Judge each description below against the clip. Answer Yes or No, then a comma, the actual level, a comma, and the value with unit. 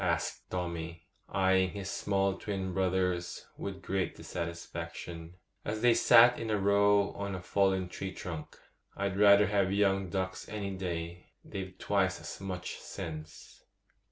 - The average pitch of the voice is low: Yes, very low, 95 Hz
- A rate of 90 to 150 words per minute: Yes, average, 140 wpm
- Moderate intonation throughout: No, narrow, 2.2 semitones